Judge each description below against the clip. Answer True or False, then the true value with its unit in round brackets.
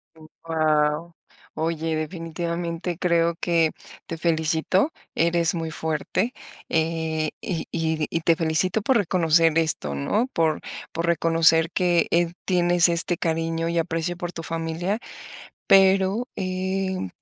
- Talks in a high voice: False (165 Hz)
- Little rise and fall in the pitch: True (1.5 semitones)